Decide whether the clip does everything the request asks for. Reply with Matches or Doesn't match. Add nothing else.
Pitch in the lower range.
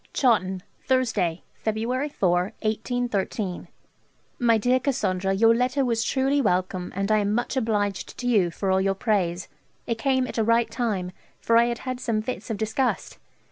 Doesn't match